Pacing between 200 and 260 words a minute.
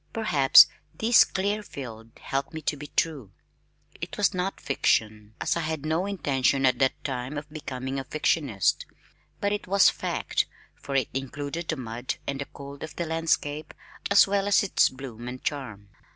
No: average, 170 wpm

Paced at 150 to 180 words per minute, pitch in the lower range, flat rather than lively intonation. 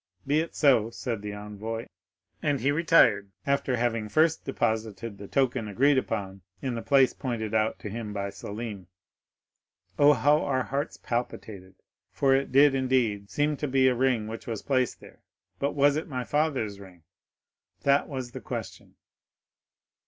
No: average, 160 wpm; low, 120 Hz; average, 4.5 semitones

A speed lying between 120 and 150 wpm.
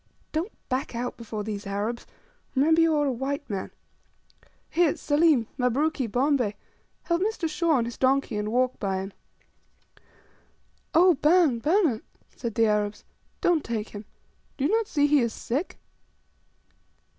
Yes: average, 145 wpm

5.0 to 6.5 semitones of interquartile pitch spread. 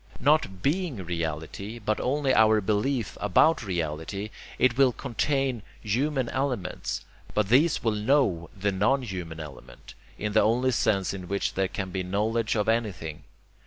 Yes: wide, 5.4 semitones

